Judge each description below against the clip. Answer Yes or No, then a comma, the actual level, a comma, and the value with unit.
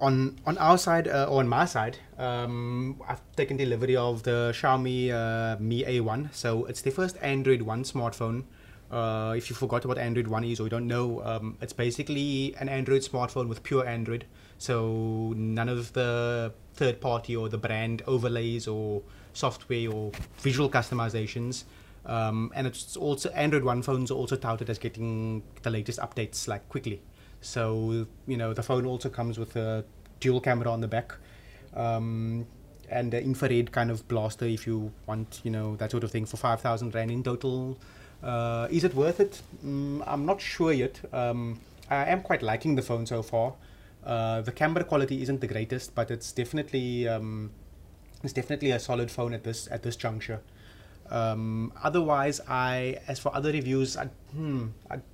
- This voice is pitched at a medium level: No, low, 120 Hz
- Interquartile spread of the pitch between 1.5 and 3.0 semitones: Yes, average, 2.7 semitones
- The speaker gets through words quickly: No, average, 180 wpm